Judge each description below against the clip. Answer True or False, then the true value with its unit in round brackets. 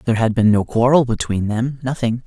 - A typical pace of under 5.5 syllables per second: False (5.8 syllables/s)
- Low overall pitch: True (120 Hz)